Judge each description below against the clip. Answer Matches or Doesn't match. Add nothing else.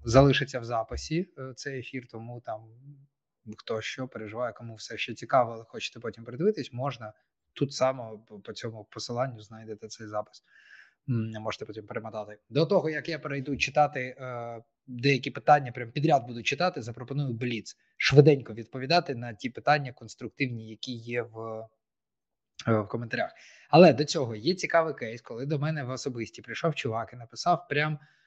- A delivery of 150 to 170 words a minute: Matches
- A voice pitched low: Matches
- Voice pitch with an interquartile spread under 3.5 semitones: Doesn't match